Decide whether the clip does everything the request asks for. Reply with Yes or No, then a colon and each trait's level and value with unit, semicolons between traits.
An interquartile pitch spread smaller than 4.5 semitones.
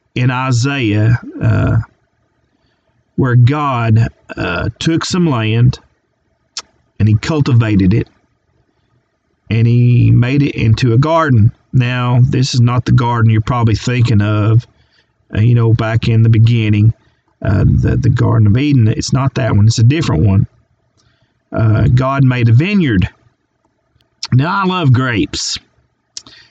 Yes: average, 2.7 semitones